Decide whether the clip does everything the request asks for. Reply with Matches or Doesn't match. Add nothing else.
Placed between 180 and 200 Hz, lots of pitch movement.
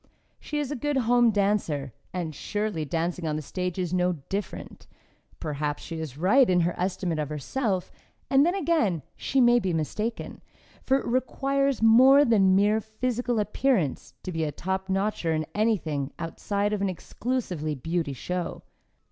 Matches